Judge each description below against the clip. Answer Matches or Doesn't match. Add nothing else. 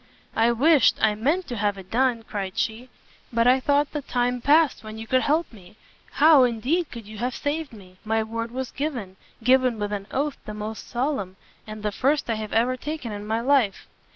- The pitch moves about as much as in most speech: Matches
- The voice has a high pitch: Matches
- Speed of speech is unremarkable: Doesn't match